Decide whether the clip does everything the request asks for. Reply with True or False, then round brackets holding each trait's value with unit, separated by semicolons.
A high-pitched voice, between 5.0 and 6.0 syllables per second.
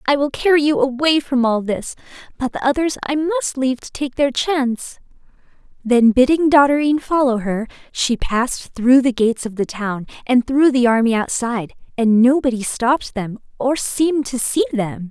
True (255 Hz; 5.1 syllables/s)